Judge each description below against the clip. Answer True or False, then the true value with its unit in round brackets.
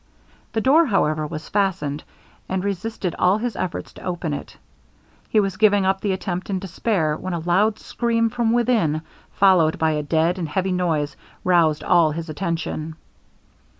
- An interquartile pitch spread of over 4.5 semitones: False (4.2 semitones)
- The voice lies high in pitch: False (180 Hz)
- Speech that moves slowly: False (165 wpm)